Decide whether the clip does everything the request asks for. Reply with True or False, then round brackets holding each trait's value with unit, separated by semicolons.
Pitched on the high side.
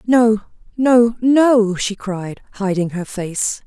True (215 Hz)